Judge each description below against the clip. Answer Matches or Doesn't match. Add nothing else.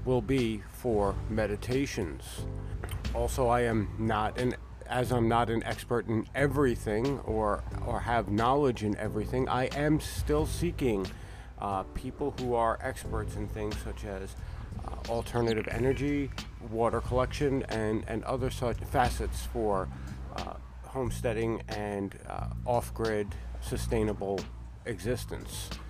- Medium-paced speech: Doesn't match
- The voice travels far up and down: Doesn't match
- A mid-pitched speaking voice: Doesn't match